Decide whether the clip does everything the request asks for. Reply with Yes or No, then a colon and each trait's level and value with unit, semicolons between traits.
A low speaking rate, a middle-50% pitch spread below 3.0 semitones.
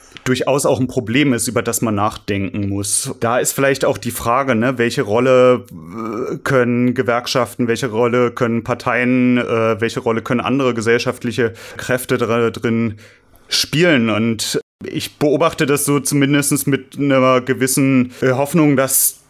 No: average, 140 wpm; narrow, 2.4 semitones